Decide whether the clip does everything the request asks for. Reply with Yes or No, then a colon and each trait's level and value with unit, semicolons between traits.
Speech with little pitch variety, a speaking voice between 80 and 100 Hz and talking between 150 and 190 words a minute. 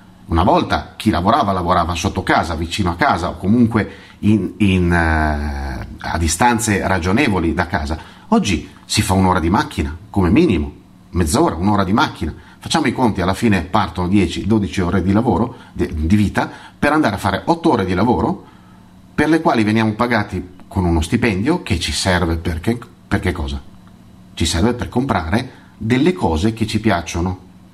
No: average, 4.0 semitones; very low, 95 Hz; fast, 170 wpm